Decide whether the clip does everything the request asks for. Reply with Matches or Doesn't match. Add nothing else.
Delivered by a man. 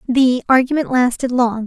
Doesn't match